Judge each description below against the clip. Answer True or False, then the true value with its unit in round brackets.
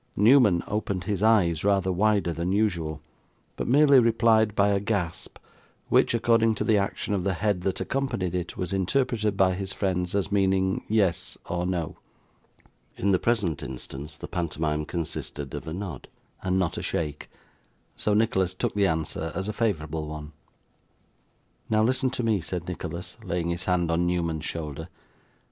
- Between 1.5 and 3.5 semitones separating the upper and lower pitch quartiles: False (3.9 semitones)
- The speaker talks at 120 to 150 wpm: False (165 wpm)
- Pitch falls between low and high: False (95 Hz)